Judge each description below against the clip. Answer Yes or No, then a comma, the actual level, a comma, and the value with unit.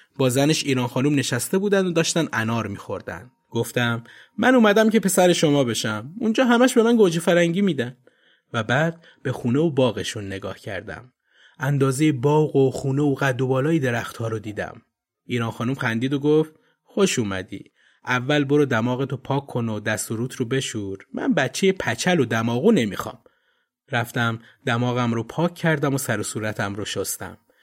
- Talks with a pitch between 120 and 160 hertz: Yes, low, 135 Hz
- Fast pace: Yes, fast, 170 wpm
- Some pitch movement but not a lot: No, wide, 5.7 semitones